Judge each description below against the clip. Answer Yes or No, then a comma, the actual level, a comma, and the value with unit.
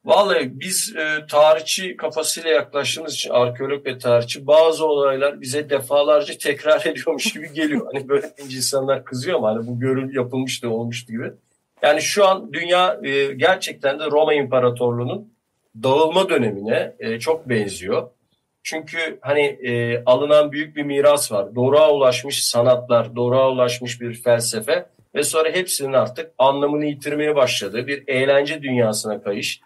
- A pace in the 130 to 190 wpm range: Yes, average, 135 wpm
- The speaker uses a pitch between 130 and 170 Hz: Yes, medium, 140 Hz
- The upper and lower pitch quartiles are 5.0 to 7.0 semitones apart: No, average, 3.7 semitones